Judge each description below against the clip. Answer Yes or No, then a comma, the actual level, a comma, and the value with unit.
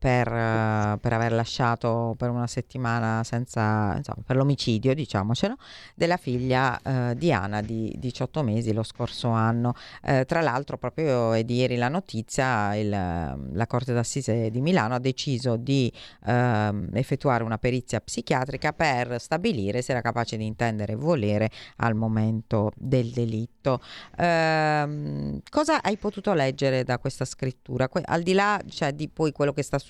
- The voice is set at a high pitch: No, low, 125 Hz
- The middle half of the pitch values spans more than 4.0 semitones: No, average, 3.5 semitones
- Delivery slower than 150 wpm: No, average, 155 wpm